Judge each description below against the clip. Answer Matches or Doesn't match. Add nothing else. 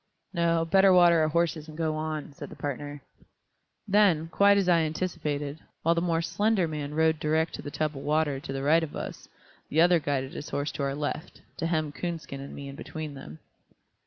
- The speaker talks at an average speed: Doesn't match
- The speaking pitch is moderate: Matches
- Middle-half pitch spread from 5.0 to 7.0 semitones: Doesn't match